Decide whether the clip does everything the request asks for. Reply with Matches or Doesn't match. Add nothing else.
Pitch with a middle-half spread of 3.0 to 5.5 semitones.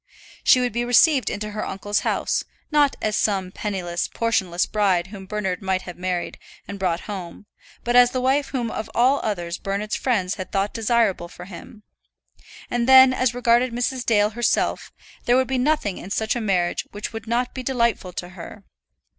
Matches